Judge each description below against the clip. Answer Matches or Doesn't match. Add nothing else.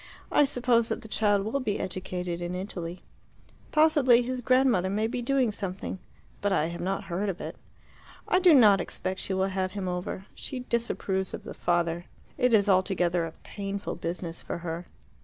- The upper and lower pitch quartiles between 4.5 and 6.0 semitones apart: Matches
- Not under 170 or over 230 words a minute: Matches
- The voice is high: Matches